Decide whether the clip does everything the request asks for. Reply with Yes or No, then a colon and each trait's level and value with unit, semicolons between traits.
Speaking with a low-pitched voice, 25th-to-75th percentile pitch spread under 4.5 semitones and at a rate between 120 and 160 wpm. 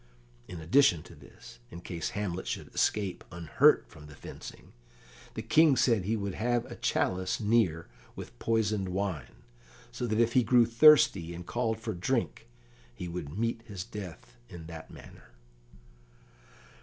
No: low, 100 Hz; average, 4.9 semitones; average, 155 wpm